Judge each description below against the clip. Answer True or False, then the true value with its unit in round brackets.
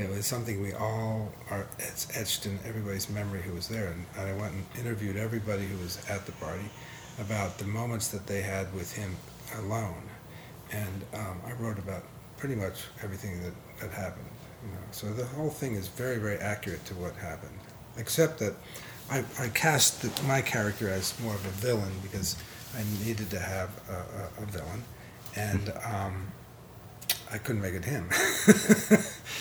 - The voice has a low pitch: True (105 Hz)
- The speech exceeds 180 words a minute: False (175 wpm)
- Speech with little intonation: False (3.7 semitones)